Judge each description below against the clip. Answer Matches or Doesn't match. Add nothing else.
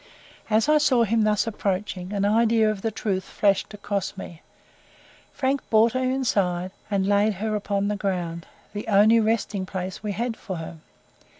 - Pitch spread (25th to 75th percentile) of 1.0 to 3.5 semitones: Matches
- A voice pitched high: Matches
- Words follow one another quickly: Doesn't match